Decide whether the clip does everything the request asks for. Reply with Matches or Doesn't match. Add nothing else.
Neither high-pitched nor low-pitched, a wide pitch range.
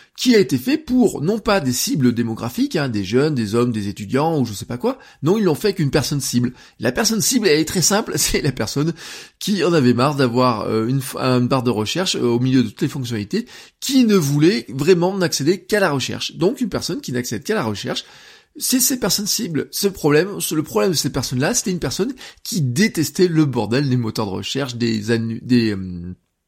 Matches